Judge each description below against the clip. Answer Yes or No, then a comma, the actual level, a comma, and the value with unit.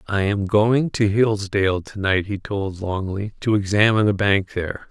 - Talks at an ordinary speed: Yes, average, 185 wpm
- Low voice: Yes, low, 100 Hz